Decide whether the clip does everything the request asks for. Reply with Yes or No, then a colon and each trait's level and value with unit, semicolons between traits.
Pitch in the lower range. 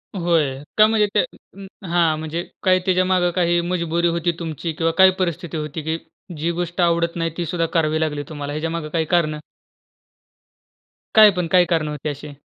No: medium, 170 Hz